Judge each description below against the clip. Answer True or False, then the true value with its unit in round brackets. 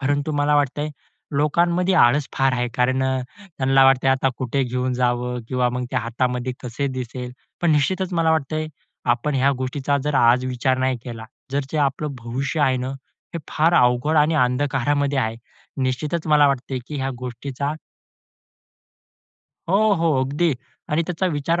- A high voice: False (135 Hz)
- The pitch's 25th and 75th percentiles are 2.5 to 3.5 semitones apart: True (3.0 semitones)